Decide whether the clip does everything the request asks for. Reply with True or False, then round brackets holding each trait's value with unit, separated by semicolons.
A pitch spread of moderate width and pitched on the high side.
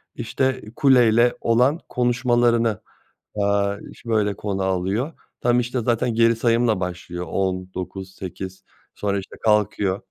False (3.9 semitones; 110 Hz)